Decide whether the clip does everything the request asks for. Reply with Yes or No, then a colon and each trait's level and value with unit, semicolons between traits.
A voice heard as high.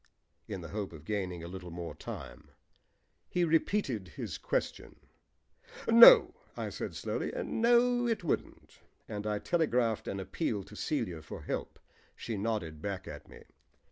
No: low, 105 Hz